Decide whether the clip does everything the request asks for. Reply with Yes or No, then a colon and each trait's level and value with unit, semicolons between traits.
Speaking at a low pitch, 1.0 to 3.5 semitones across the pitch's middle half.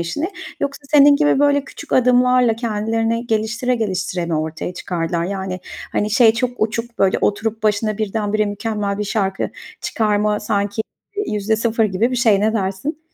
No: high, 215 Hz; average, 2.9 semitones